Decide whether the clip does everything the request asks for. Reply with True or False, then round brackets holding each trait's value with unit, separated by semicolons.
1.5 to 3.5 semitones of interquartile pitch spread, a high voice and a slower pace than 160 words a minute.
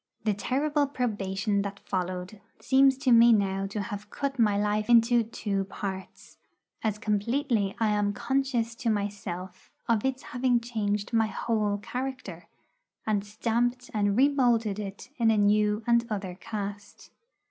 True (2.9 semitones; 215 Hz; 145 wpm)